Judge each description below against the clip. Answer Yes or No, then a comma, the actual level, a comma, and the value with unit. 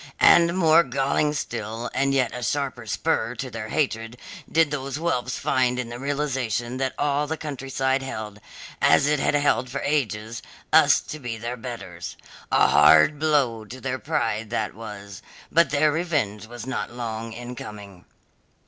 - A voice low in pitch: Yes, low, 125 Hz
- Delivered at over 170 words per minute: No, average, 165 wpm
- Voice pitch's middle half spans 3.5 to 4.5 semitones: Yes, average, 4.1 semitones